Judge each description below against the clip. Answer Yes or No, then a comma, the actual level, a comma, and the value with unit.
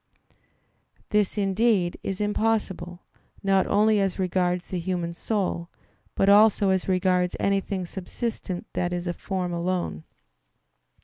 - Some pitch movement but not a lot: No, narrow, 2.2 semitones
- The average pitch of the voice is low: No, high, 190 Hz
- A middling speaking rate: No, slow, 125 wpm